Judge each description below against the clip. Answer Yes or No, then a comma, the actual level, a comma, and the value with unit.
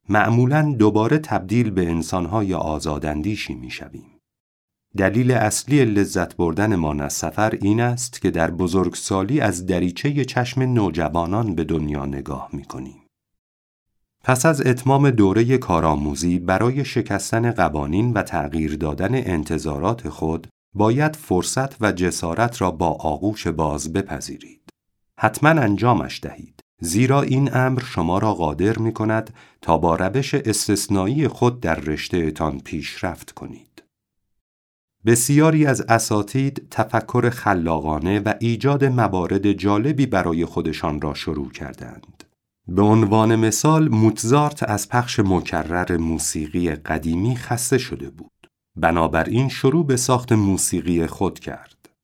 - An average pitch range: No, wide, 6.5 semitones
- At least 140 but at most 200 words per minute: No, average, 120 wpm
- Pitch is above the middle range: No, low, 100 Hz